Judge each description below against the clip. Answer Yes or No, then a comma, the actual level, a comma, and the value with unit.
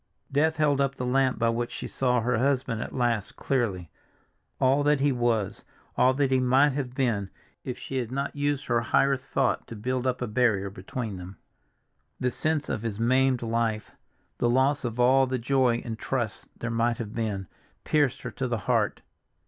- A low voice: Yes, low, 125 Hz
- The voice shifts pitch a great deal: No, narrow, 2.6 semitones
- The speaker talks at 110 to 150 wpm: No, average, 190 wpm